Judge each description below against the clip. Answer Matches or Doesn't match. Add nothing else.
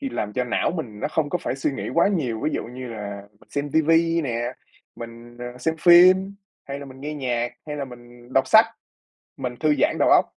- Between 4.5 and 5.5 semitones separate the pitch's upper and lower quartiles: Matches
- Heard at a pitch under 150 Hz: Matches